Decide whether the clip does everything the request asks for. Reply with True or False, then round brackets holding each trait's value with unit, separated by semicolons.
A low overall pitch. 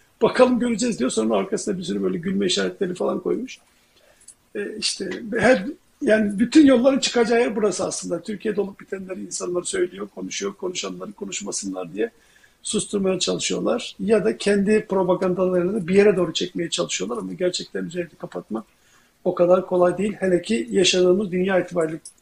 False (190 Hz)